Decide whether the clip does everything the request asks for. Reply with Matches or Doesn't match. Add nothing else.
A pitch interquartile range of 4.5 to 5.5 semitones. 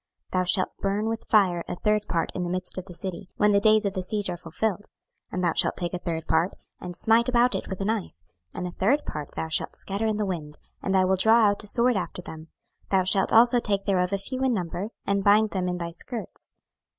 Doesn't match